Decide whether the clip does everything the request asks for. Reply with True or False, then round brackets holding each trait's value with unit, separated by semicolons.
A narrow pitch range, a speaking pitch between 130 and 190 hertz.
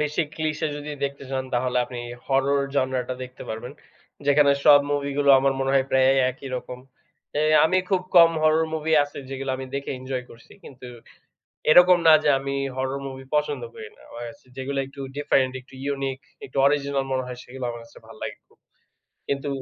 True (1.9 semitones; 135 Hz)